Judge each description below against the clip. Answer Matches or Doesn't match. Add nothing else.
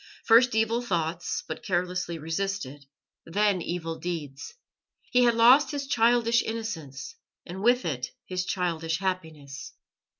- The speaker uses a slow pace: Matches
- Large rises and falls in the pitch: Matches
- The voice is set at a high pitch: Doesn't match